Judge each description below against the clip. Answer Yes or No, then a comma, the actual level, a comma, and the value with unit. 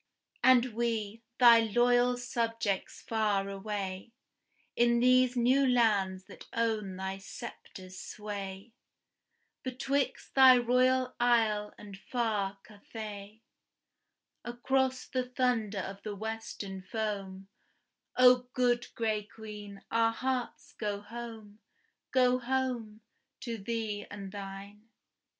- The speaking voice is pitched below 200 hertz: No, high, 225 Hz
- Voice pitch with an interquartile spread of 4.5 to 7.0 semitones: No, average, 3.3 semitones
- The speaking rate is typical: No, slow, 105 wpm